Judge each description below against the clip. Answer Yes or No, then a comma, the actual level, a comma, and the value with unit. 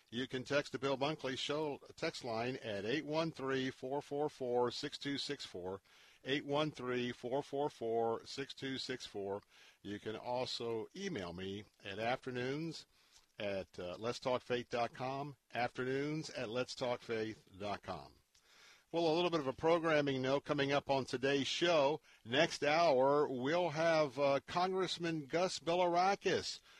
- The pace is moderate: No, slow, 105 wpm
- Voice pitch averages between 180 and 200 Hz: No, low, 135 Hz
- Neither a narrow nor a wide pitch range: Yes, average, 3.5 semitones